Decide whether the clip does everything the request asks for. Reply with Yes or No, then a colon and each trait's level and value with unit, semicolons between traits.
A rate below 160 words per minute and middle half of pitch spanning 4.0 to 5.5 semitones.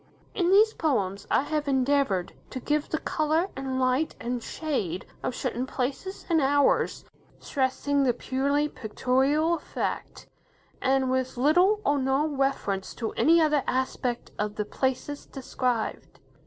No: average, 140 wpm; average, 3.1 semitones